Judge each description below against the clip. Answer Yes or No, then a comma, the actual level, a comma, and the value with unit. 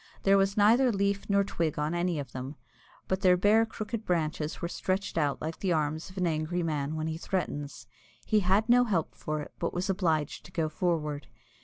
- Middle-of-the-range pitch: Yes, medium, 175 Hz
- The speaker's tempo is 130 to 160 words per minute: No, fast, 205 wpm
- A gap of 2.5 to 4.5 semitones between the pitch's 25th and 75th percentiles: Yes, average, 4.2 semitones